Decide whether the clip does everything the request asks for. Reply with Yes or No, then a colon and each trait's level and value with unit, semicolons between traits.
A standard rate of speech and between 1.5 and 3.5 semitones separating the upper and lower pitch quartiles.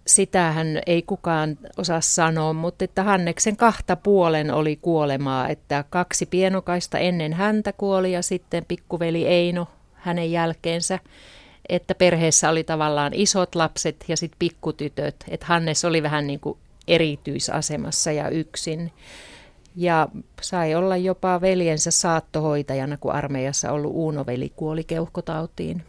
Yes: average, 125 wpm; narrow, 2.5 semitones